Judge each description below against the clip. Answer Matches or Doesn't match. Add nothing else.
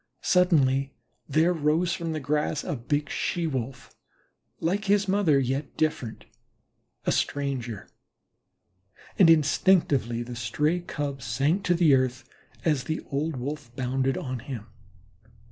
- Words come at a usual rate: Doesn't match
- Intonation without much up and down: Doesn't match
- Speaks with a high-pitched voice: Doesn't match